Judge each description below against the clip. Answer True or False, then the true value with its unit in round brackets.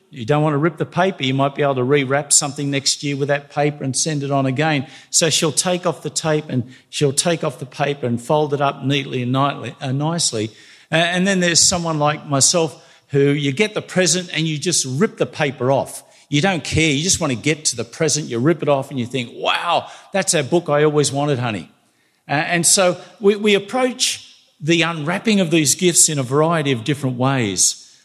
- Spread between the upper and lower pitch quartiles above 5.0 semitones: False (3.6 semitones)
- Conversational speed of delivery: False (220 wpm)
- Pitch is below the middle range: False (150 Hz)